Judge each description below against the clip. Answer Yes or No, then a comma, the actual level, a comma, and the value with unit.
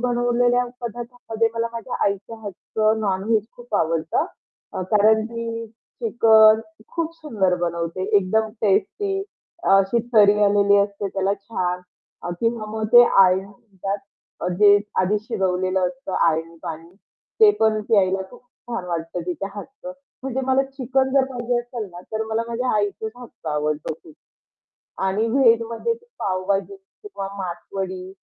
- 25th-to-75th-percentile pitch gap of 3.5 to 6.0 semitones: Yes, average, 4.0 semitones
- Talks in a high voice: Yes, high, 215 Hz